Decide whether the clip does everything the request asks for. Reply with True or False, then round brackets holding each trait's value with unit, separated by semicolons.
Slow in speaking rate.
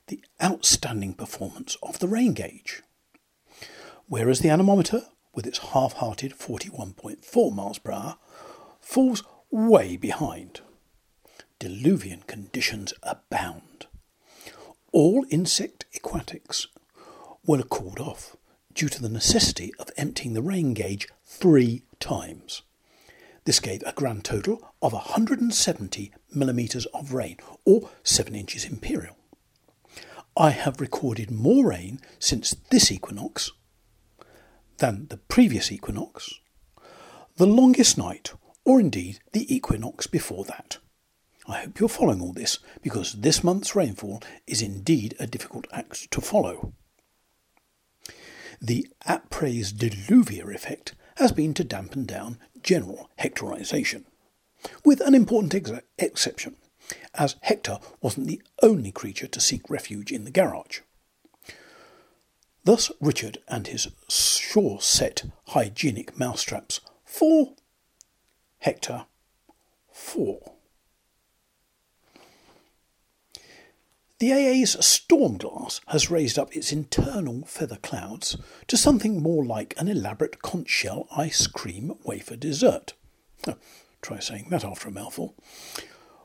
True (110 wpm)